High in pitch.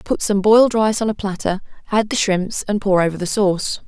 Yes: high, 200 Hz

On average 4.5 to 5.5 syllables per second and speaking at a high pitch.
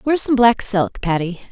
Yes: 5.2 syllables/s; high, 210 Hz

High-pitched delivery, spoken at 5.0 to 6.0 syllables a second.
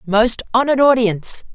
Yes: high, 230 Hz; 5.6 syllables/s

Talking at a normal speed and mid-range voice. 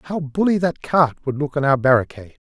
No: fast, 220 wpm; medium, 145 Hz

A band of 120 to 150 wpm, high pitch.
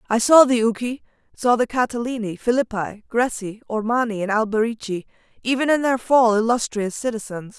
Yes: average, 140 wpm; high, 230 Hz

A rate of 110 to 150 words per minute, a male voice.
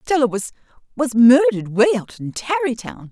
No: slow, 135 wpm; female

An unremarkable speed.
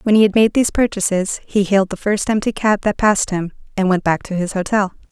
No: fast, 245 wpm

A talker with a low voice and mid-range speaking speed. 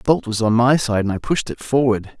No: low, 120 Hz; fast, 300 wpm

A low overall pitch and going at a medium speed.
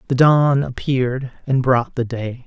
Yes: low, 130 Hz; average, 170 wpm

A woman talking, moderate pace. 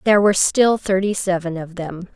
Yes: female; average, 195 wpm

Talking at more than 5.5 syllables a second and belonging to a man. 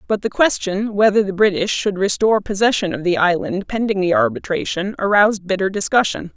No: 5.7 syllables/s; female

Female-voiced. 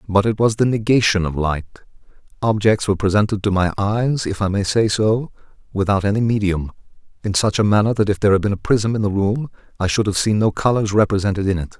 No: male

